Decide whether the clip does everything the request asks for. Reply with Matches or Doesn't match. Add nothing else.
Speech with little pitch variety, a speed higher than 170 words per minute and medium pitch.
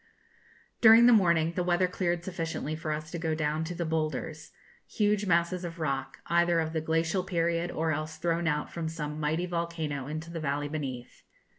Matches